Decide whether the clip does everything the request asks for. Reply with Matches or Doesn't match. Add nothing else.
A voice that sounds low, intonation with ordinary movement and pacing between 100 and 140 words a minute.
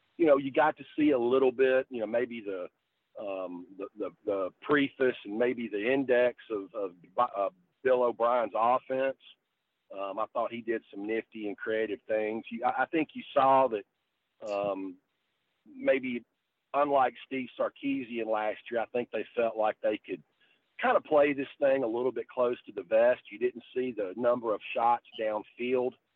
Doesn't match